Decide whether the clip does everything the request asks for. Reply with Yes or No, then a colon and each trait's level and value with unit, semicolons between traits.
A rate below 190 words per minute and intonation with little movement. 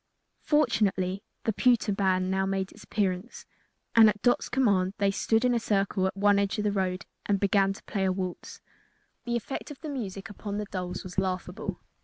No: average, 195 wpm; narrow, 2.3 semitones